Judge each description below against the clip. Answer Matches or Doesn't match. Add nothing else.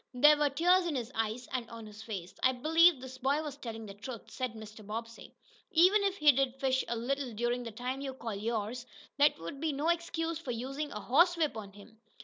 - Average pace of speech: Doesn't match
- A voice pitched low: Doesn't match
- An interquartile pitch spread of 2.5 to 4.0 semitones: Doesn't match